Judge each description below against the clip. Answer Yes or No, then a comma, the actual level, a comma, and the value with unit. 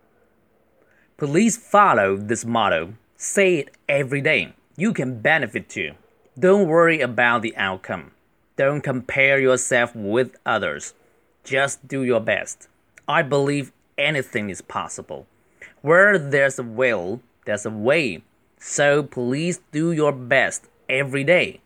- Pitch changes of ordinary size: Yes, average, 4.9 semitones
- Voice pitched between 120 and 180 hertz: Yes, medium, 140 Hz